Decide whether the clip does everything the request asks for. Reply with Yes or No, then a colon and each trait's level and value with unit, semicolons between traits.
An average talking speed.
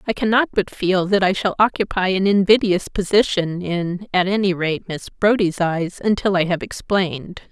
Yes: average, 175 wpm